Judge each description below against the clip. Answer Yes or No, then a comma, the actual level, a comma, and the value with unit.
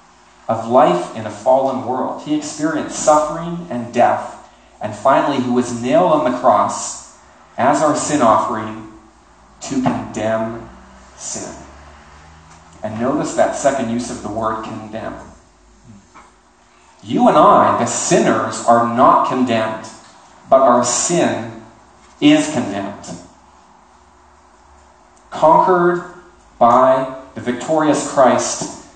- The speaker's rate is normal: No, slow, 110 wpm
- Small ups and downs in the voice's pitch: No, average, 3.7 semitones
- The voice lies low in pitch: Yes, low, 115 Hz